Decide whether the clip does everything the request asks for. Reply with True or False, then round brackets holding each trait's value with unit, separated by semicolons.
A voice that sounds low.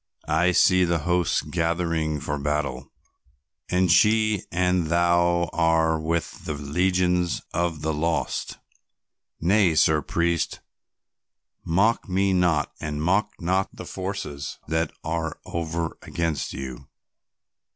True (85 Hz)